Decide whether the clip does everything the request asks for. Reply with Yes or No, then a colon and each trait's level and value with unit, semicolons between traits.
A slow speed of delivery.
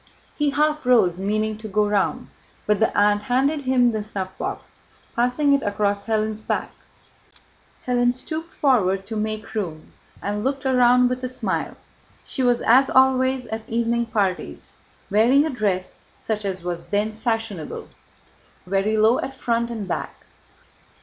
No: average, 150 wpm